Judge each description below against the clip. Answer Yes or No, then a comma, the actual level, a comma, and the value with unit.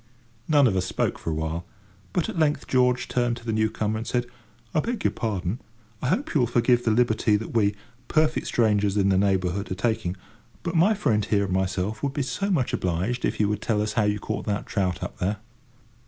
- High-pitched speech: No, low, 110 Hz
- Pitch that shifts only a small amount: No, average, 3.9 semitones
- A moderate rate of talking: No, fast, 220 wpm